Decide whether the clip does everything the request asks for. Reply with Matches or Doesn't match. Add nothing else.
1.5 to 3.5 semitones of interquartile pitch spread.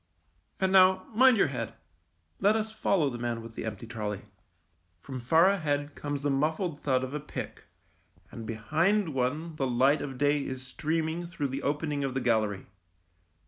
Doesn't match